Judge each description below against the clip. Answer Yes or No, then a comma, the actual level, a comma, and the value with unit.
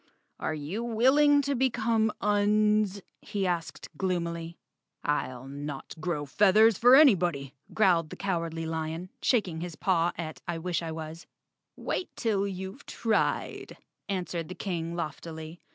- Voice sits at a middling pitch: Yes, medium, 180 Hz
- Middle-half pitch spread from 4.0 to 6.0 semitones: Yes, average, 4.6 semitones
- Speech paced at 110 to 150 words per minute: Yes, slow, 135 wpm